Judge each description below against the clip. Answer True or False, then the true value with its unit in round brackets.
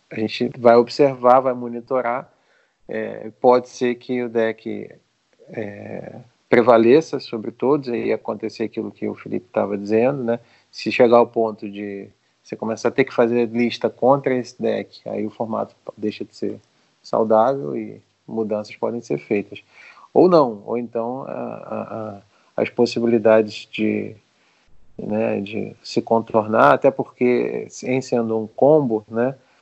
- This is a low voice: True (115 Hz)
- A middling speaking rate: True (150 wpm)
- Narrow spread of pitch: True (1.9 semitones)